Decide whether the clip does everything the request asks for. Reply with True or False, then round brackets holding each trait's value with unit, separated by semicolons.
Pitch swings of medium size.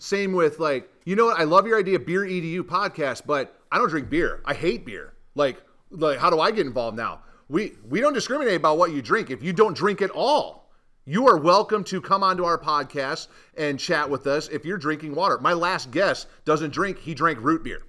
True (4.2 semitones)